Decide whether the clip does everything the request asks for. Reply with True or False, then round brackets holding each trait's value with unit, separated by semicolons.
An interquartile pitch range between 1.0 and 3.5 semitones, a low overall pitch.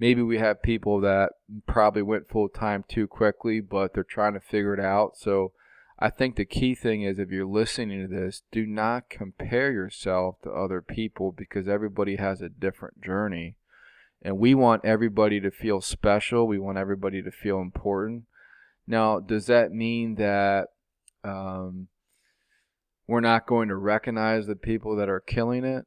True (2.6 semitones; 105 Hz)